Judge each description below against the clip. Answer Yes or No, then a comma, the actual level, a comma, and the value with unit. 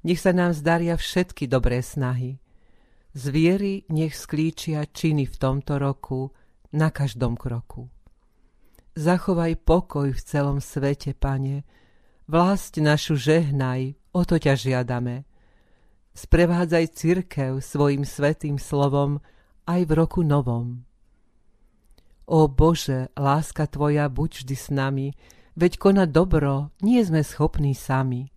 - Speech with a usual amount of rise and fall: Yes, average, 3.5 semitones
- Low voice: No, medium, 145 Hz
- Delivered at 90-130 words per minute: Yes, average, 115 wpm